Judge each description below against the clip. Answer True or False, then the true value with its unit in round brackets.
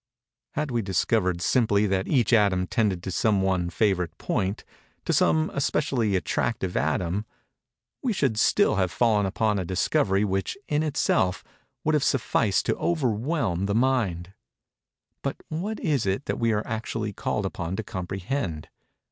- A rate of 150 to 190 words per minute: False (140 wpm)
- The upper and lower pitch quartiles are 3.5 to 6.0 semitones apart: True (4.9 semitones)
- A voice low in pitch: True (105 Hz)